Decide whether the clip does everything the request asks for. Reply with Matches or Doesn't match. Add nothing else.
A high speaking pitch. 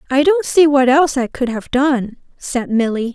Matches